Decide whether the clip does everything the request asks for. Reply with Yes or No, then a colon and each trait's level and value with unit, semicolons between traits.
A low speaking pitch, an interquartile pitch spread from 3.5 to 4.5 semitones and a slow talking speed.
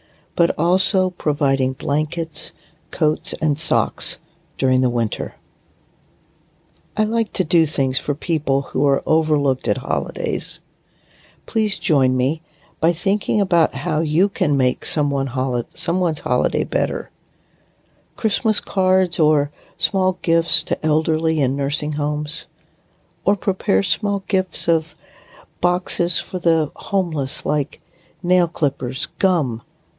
No: medium, 160 Hz; average, 4.2 semitones; slow, 115 wpm